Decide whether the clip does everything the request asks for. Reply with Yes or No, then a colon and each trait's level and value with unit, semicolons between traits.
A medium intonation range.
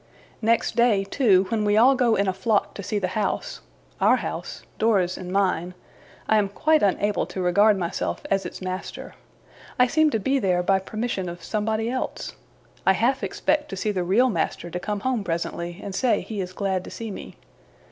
Yes: average, 3.6 semitones